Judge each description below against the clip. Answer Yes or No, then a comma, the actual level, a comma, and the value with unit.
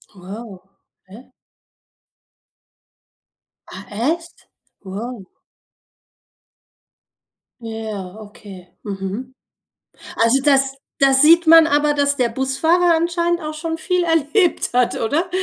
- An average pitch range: No, wide, 6.8 semitones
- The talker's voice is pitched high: Yes, very high, 270 Hz